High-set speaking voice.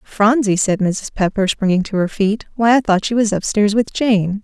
Yes: high, 210 Hz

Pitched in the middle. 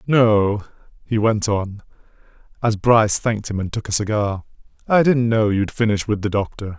No: low, 110 Hz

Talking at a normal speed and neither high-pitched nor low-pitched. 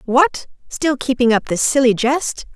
No: average, 165 wpm; very high, 260 Hz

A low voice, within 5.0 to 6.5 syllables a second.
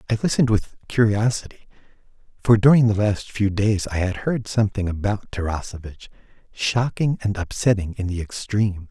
Yes: low, 105 Hz; 5.4 syllables/s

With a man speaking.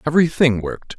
Yes: male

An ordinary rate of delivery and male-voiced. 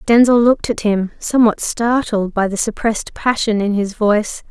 No: average, 175 wpm; female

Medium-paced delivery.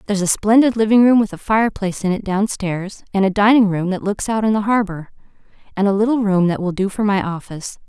No: fast, 235 wpm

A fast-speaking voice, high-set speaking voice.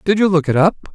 No: fast, 320 wpm; medium, 175 Hz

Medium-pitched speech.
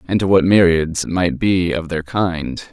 No: very low, 85 Hz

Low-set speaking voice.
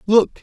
No: high, 215 Hz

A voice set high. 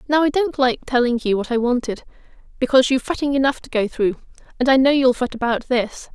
Yes: very high, 255 Hz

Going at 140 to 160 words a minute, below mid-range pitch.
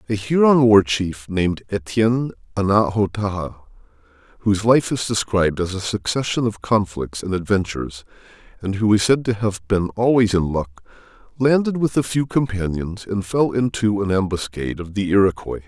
Yes: average, 155 wpm; low, 100 Hz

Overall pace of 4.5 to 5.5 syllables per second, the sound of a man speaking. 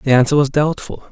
No: 5.7 syllables/s; male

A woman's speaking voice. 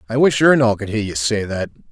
No: male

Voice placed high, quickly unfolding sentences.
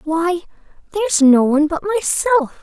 No: very high, 340 Hz; slow, 135 wpm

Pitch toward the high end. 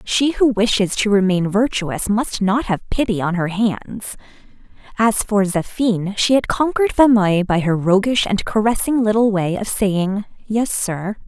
Yes: high, 210 Hz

